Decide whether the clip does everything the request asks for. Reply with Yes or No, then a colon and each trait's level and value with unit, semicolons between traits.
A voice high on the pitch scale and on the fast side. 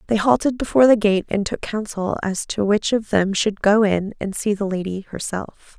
Yes: high, 205 Hz; fast, 220 wpm